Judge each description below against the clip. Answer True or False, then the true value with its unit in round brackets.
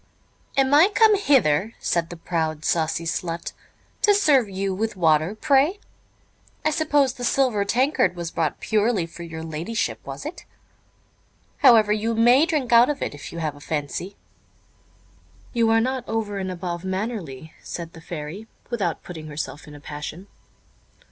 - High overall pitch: True (200 Hz)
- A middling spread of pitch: False (7.0 semitones)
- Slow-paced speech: False (160 wpm)